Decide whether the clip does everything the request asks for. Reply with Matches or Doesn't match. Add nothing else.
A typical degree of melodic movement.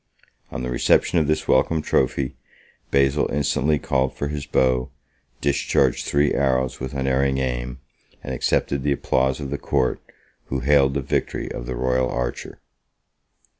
Doesn't match